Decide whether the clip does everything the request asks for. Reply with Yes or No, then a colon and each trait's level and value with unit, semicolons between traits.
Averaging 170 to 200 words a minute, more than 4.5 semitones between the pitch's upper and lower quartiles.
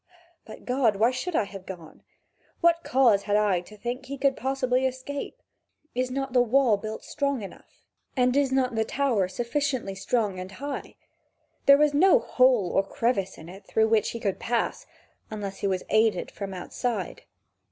Yes: average, 180 wpm; average, 4.9 semitones